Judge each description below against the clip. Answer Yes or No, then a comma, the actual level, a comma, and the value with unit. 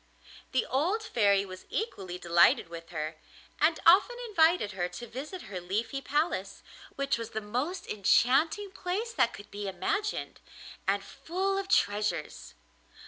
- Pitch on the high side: Yes, high, 240 Hz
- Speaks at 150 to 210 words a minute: No, average, 140 wpm